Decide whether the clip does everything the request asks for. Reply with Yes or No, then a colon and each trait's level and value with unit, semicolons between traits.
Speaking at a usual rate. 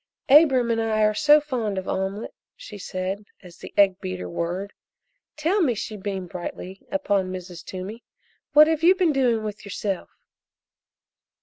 Yes: average, 160 wpm